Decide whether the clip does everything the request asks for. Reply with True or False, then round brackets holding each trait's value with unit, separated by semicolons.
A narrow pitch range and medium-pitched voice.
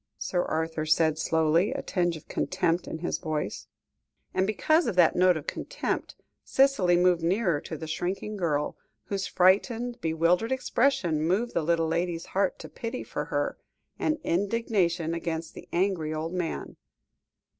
False (3.7 semitones; 175 Hz)